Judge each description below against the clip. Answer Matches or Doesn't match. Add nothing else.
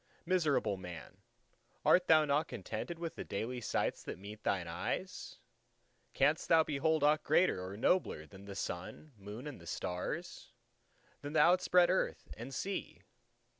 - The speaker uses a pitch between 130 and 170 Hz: Matches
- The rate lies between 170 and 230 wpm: Doesn't match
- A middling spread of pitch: Doesn't match